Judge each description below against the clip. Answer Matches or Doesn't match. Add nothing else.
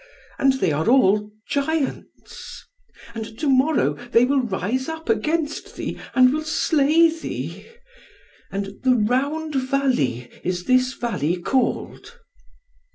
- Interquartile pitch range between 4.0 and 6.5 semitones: Matches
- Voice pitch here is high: Matches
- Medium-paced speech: Doesn't match